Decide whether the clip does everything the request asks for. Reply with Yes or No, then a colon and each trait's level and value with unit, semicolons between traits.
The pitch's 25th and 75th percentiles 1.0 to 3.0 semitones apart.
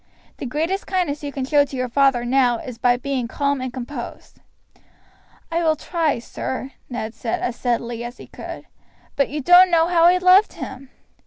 No: average, 5.0 semitones